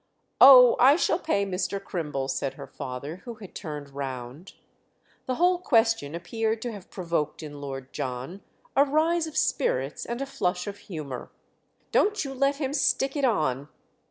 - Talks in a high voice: Yes, high, 195 Hz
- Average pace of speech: Yes, average, 165 wpm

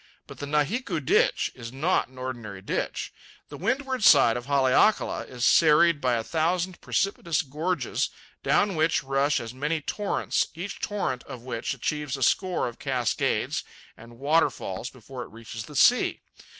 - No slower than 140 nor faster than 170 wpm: Yes, average, 155 wpm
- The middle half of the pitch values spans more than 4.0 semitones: Yes, average, 5.3 semitones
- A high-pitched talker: No, medium, 145 Hz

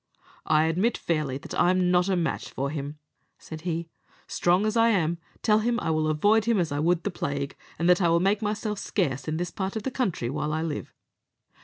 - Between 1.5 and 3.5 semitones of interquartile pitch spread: No, average, 4.8 semitones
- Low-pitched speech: No, medium, 175 Hz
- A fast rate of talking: Yes, fast, 220 wpm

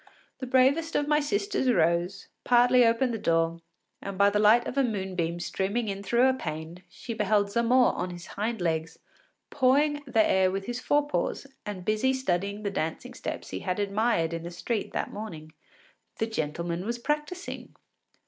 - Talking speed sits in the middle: Yes, average, 175 wpm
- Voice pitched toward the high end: Yes, high, 210 Hz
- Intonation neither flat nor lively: No, wide, 6.1 semitones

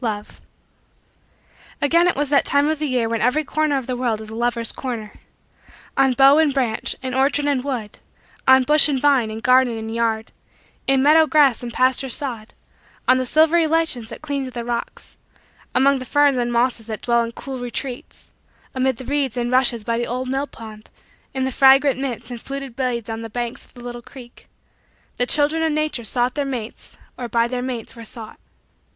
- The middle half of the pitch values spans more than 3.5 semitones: No, average, 2.9 semitones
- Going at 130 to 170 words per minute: No, average, 200 wpm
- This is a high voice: Yes, very high, 255 Hz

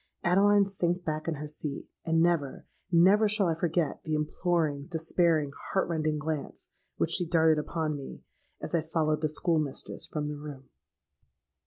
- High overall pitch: No, medium, 160 Hz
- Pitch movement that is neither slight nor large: No, narrow, 2.3 semitones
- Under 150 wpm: No, average, 160 wpm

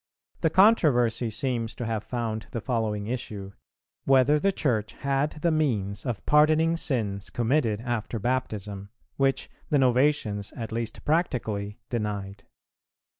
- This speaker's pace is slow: Yes, slow, 130 wpm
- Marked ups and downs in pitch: No, average, 4.7 semitones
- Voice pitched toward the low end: Yes, low, 120 Hz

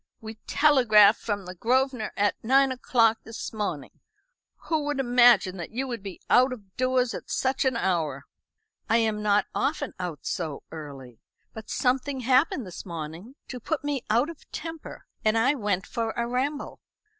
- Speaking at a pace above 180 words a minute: No, average, 170 wpm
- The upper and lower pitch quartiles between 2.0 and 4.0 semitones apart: No, average, 4.6 semitones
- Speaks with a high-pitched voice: Yes, high, 230 Hz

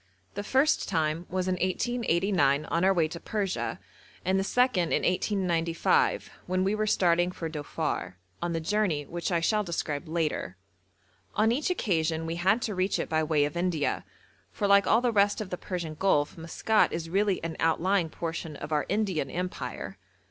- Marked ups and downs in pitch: No, average, 3.6 semitones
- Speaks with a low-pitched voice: No, medium, 180 Hz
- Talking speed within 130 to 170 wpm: No, average, 180 wpm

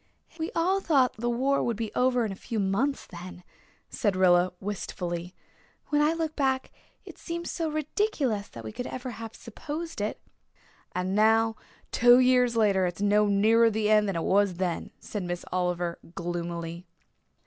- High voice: Yes, high, 215 Hz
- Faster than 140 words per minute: Yes, average, 170 wpm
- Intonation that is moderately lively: No, wide, 5.8 semitones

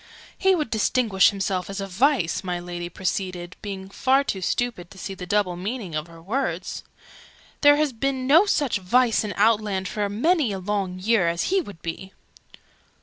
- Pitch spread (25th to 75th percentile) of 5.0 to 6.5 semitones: Yes, wide, 5.6 semitones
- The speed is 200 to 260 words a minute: No, average, 180 wpm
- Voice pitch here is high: Yes, high, 200 Hz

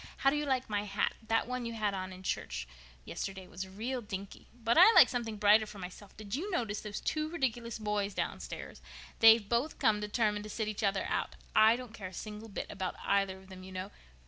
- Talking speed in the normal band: No, fast, 225 wpm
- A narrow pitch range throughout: No, average, 3.1 semitones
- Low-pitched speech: No, high, 210 Hz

